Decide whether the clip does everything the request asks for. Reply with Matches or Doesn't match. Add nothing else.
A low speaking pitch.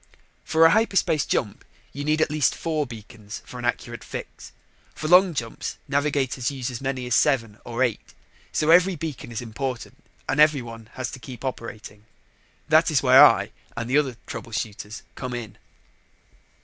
Matches